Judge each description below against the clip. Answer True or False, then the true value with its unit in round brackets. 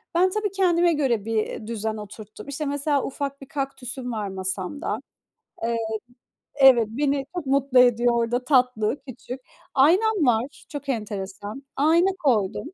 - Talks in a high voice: True (260 Hz)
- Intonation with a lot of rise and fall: False (4.4 semitones)